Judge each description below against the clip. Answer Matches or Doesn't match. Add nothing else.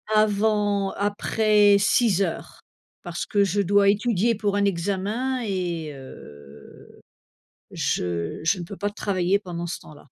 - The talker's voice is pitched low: Doesn't match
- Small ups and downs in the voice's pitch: Doesn't match